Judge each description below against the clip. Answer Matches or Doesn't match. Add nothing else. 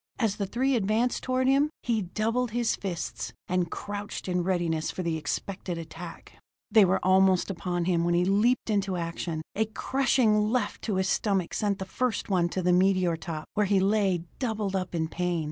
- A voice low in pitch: Doesn't match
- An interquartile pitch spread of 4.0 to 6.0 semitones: Doesn't match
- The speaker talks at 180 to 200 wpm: Matches